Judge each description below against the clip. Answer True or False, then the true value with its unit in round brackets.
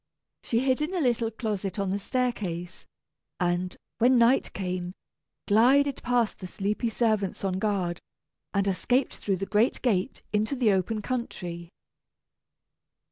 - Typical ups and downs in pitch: True (4.6 semitones)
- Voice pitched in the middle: False (210 Hz)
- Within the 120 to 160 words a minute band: True (135 wpm)